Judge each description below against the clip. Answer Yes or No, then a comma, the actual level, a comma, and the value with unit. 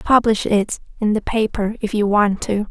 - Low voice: No, high, 210 Hz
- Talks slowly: No, average, 200 wpm